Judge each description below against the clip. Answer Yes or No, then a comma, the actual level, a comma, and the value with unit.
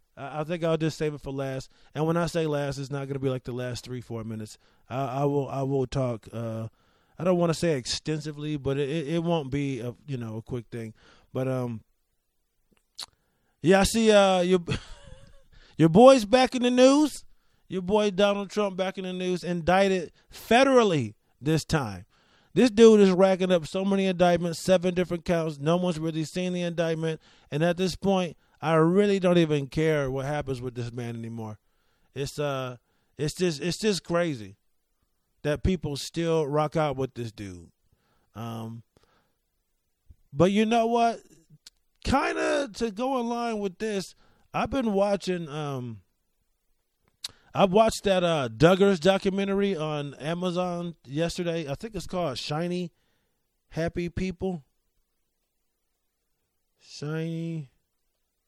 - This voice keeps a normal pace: Yes, average, 160 wpm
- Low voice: No, medium, 160 Hz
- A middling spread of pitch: No, wide, 6.3 semitones